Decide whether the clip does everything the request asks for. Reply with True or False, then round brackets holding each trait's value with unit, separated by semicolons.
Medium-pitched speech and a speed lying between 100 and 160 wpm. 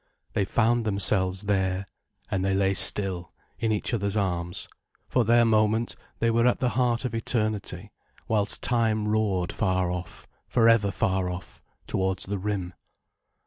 False (100 Hz; 150 wpm)